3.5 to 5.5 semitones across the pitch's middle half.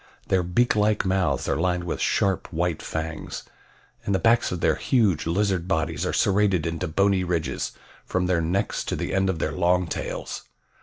No: average, 2.8 semitones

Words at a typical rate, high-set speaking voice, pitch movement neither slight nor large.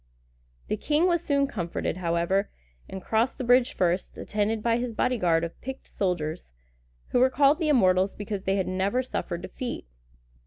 No: average, 165 wpm; high, 210 Hz; wide, 5.8 semitones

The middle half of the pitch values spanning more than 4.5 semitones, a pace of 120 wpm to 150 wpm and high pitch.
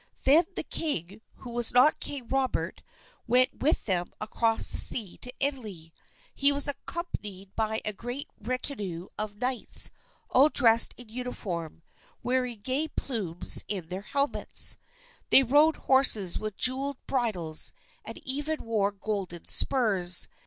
Yes: average, 5.2 semitones; slow, 135 wpm; high, 235 Hz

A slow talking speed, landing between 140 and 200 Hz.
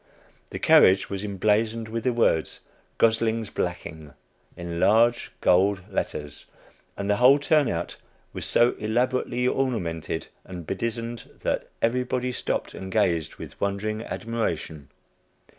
No: slow, 120 wpm; low, 110 Hz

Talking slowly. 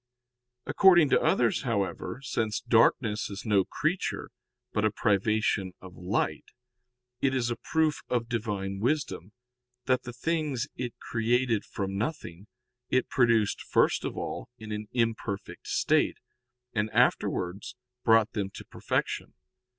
Yes: slow, 130 wpm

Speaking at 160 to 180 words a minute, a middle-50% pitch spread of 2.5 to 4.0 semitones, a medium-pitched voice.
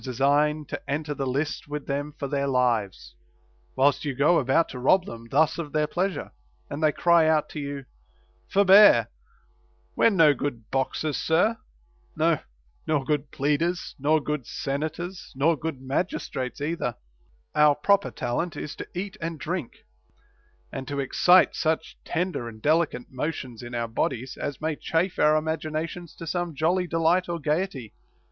Yes: average, 165 wpm; average, 3.5 semitones; medium, 150 Hz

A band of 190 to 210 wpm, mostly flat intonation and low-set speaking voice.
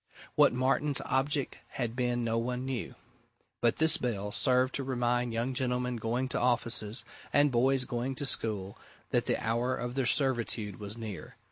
No: average, 170 wpm; narrow, 2.1 semitones; low, 125 Hz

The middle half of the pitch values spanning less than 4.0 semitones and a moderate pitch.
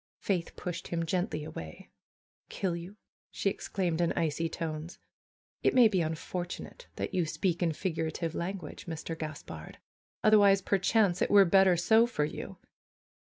Yes: average, 3.1 semitones; medium, 175 Hz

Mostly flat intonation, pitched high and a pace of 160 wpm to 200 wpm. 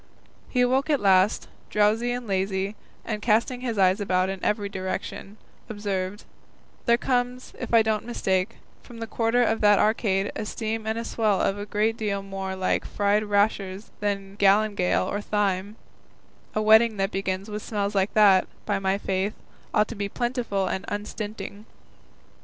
Yes: narrow, 2.3 semitones; high, 205 Hz; average, 165 wpm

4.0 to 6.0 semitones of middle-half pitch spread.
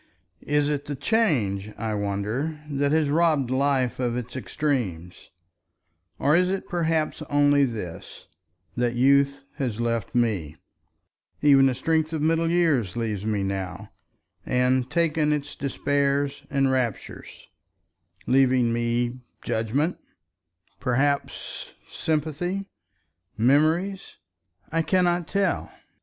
Yes: average, 4.7 semitones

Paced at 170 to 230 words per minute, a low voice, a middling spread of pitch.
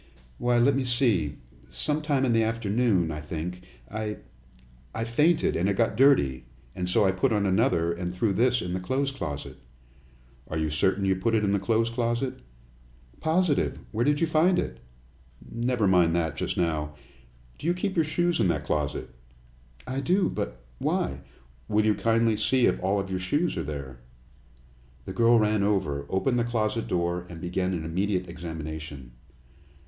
No: average, 180 wpm; low, 100 Hz; wide, 6.1 semitones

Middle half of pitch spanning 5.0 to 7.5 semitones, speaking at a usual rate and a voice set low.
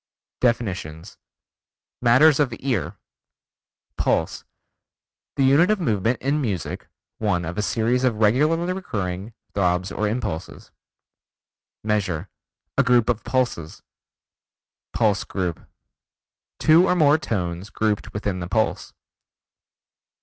No: wide, 5.6 semitones; slow, 105 wpm; low, 110 Hz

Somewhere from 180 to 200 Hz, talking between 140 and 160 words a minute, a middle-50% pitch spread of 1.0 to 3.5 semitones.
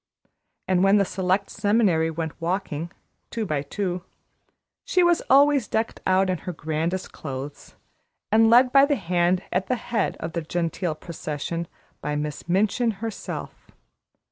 No: medium, 185 Hz; average, 145 wpm; average, 5.1 semitones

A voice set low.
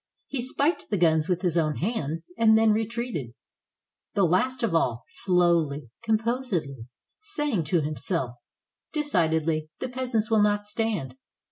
No: medium, 185 Hz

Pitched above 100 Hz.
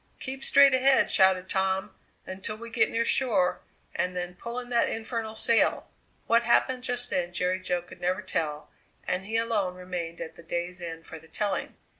Yes: high, 190 Hz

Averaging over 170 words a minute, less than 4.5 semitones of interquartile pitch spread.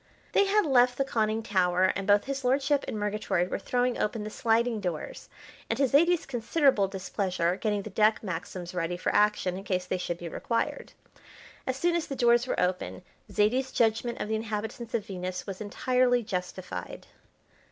No: average, 180 wpm; average, 4.9 semitones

